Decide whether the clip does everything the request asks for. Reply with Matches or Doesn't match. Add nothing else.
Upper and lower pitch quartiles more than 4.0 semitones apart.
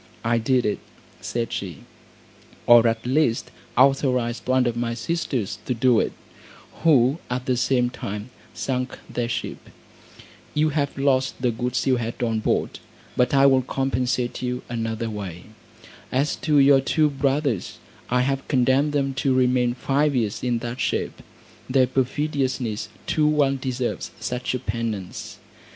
Doesn't match